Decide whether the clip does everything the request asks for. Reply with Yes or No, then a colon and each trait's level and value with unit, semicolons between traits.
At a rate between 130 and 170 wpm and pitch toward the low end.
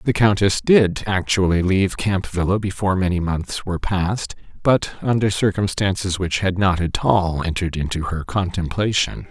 Yes: average, 155 wpm; very low, 95 Hz